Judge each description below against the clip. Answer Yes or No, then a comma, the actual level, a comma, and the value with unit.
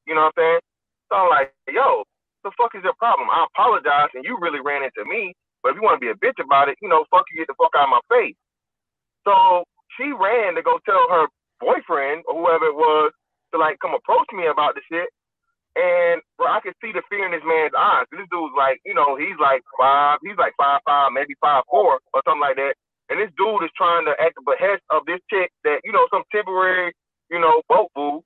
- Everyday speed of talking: No, fast, 245 wpm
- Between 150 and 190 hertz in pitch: Yes, medium, 185 Hz